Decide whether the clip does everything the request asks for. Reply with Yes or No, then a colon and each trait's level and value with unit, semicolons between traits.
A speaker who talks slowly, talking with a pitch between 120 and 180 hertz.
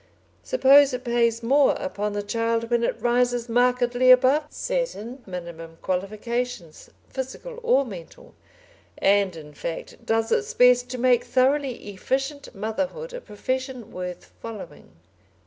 No: slow, 130 wpm; high, 245 Hz